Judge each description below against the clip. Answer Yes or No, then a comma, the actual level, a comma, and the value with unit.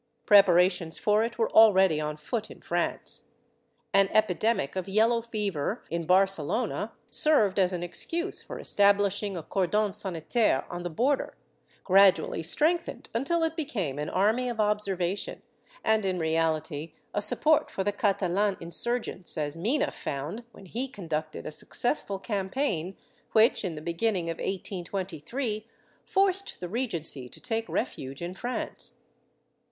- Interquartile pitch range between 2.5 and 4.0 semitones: No, average, 4.8 semitones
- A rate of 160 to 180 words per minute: No, average, 145 wpm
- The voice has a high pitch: Yes, high, 195 Hz